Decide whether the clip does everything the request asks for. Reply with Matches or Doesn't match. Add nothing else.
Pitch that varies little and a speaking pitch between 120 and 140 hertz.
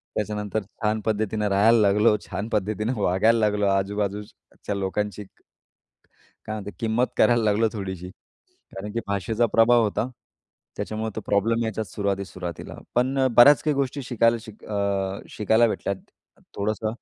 Doesn't match